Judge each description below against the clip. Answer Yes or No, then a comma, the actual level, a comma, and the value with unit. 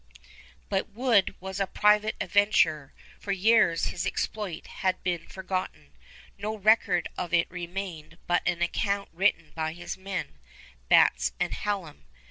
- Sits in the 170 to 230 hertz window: Yes, medium, 185 Hz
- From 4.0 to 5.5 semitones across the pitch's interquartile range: No, average, 3.3 semitones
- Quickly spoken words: No, slow, 135 wpm